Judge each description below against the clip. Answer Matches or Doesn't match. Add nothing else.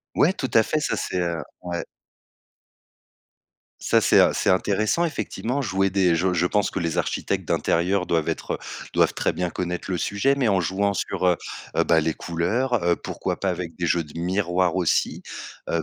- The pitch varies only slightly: Doesn't match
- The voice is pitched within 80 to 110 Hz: Matches